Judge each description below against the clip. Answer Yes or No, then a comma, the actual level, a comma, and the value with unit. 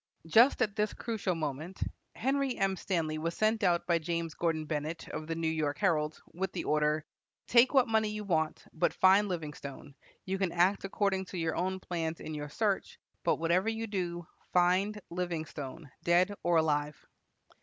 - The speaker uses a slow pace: No, average, 175 wpm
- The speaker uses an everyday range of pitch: Yes, average, 3.9 semitones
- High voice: No, medium, 175 Hz